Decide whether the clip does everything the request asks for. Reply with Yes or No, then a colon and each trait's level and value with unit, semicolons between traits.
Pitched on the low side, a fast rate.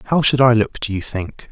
Yes: low, 115 Hz; fast, 275 wpm